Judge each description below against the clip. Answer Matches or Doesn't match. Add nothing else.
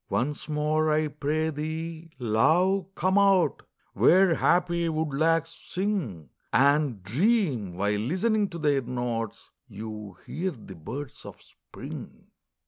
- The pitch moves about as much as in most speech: Doesn't match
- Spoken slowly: Matches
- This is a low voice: Doesn't match